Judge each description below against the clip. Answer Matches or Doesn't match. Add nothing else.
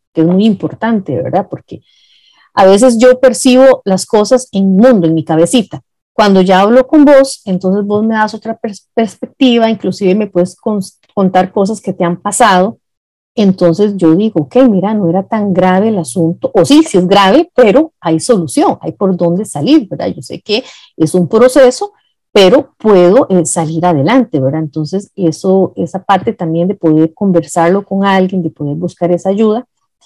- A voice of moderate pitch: Doesn't match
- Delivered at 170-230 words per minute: Matches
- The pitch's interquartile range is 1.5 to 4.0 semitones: Doesn't match